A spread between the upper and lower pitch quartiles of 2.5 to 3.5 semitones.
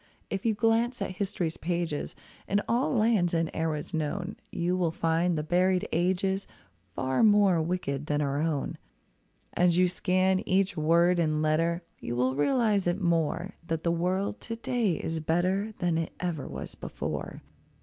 Yes: average, 3.1 semitones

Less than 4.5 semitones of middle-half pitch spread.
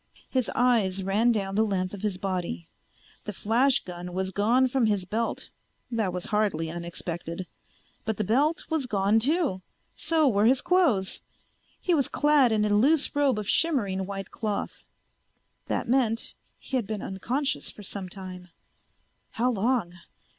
No: average, 5.1 semitones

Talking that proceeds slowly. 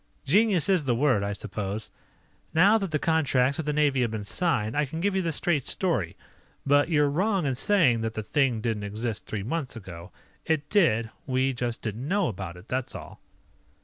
No: average, 200 wpm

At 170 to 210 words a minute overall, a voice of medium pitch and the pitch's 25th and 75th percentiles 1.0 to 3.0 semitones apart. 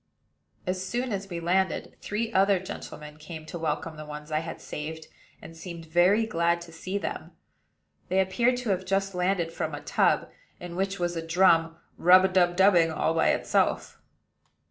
Yes: average, 180 wpm; medium, 175 Hz; average, 2.7 semitones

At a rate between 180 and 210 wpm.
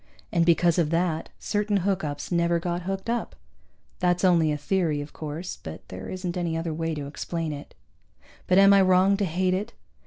Yes: average, 190 wpm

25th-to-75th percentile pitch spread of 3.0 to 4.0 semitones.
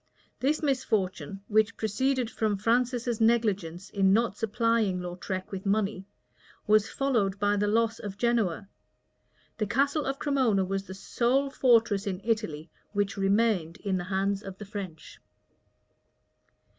Yes: average, 3.3 semitones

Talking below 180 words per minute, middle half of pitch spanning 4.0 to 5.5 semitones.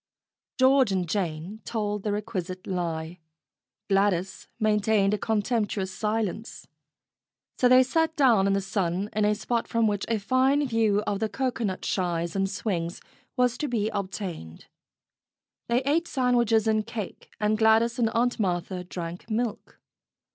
No: average, 145 wpm; average, 3.5 semitones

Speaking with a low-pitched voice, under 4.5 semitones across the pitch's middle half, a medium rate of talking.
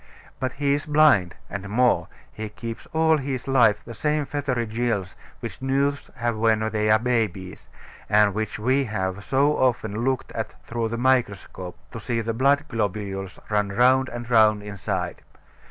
Yes: low, 115 Hz; average, 3.9 semitones; average, 165 wpm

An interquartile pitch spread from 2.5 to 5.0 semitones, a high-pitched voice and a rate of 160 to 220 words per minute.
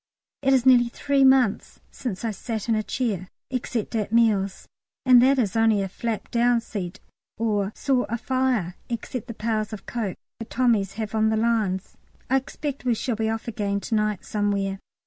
Yes: average, 3.0 semitones; high, 225 Hz; average, 185 wpm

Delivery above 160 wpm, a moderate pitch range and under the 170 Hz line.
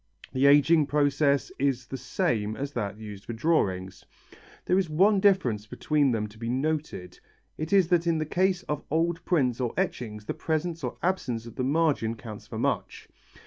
No: average, 185 wpm; wide, 6.1 semitones; medium, 140 Hz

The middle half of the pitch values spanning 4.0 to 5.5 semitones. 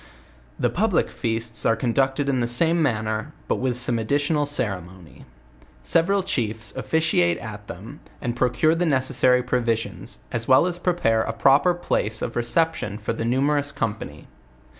Yes: average, 4.6 semitones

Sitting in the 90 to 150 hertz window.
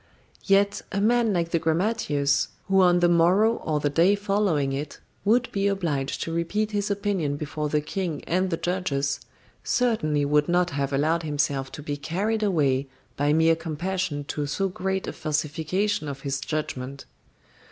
No: medium, 165 Hz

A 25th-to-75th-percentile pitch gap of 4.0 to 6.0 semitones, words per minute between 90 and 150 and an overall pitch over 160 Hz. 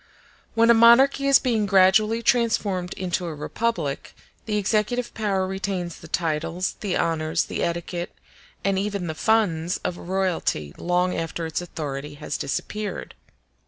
Yes: average, 4.3 semitones; average, 140 wpm; medium, 185 Hz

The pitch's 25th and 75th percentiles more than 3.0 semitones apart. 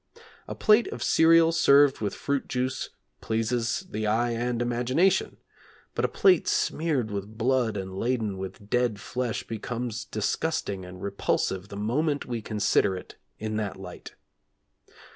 Yes: average, 4.2 semitones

